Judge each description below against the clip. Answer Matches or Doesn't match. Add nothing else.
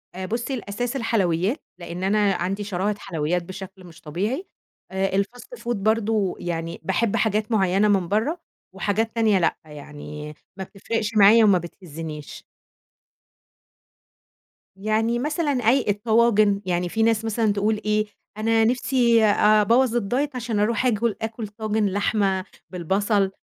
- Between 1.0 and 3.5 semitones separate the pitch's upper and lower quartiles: Matches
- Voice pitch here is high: Matches